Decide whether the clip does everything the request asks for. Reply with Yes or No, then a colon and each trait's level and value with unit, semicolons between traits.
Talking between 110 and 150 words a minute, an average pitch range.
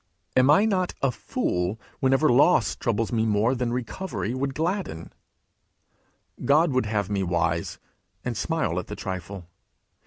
No: average, 145 wpm; wide, 5.8 semitones